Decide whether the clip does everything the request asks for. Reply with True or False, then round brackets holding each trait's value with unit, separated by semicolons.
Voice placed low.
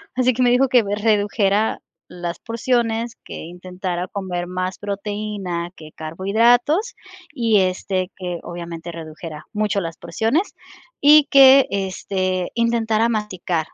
False (200 Hz)